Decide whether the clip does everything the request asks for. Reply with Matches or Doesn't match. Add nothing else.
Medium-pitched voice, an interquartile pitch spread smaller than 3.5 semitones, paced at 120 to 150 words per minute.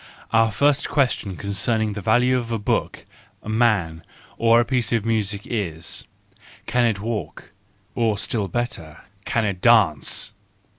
Doesn't match